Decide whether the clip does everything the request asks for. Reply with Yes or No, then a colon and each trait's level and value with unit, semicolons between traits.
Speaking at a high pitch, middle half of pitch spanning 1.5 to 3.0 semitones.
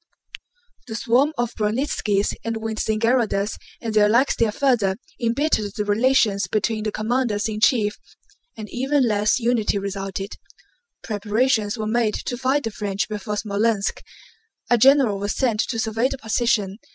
Yes: high, 220 Hz; narrow, 2.6 semitones